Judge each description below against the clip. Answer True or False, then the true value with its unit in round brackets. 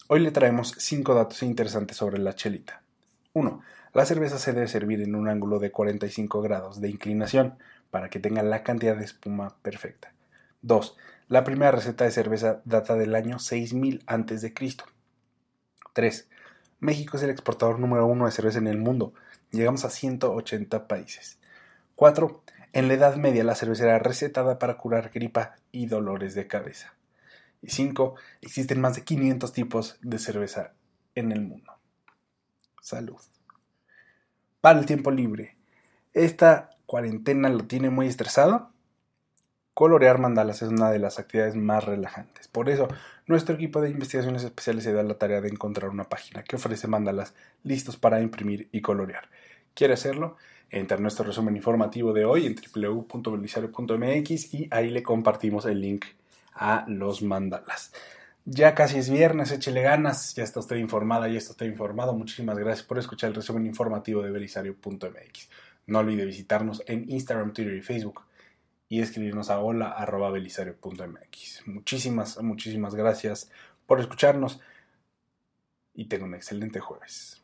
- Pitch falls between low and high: False (115 Hz)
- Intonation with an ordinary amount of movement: True (3.5 semitones)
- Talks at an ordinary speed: True (150 wpm)